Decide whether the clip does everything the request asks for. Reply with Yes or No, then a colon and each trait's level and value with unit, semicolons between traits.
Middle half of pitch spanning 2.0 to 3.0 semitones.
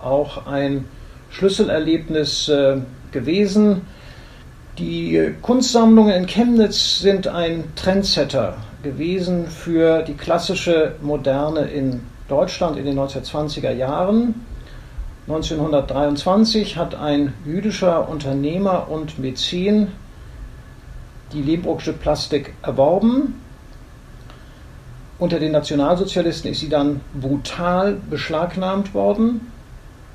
No: average, 4.9 semitones